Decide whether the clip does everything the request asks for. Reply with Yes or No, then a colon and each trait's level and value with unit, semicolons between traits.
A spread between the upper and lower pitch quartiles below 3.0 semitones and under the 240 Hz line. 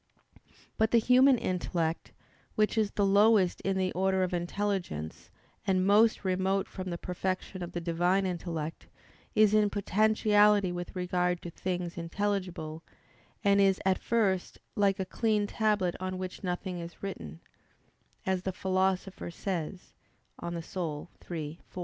Yes: narrow, 2.4 semitones; medium, 185 Hz